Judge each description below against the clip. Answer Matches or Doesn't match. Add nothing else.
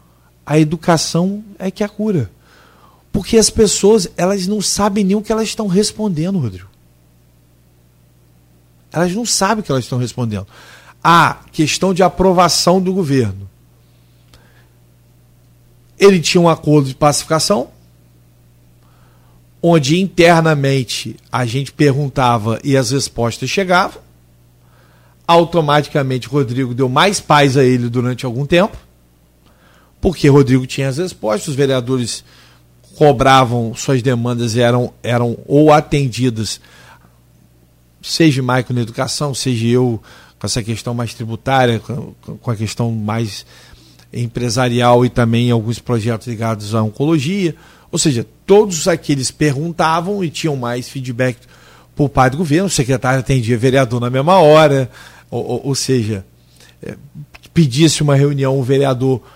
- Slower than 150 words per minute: Matches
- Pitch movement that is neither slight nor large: Doesn't match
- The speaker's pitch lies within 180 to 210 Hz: Doesn't match